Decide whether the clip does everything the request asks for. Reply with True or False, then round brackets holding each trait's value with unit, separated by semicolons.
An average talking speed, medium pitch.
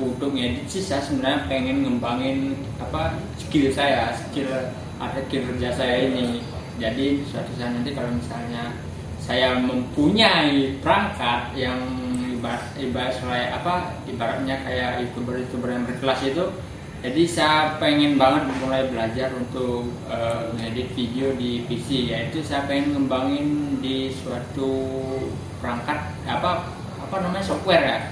False (130 wpm; 130 Hz)